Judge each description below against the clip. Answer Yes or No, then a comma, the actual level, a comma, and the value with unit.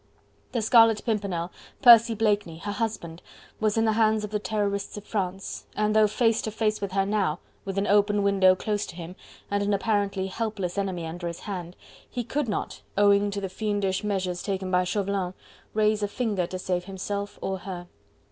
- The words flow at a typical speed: Yes, average, 190 wpm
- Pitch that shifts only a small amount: Yes, narrow, 2.3 semitones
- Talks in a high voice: Yes, high, 200 Hz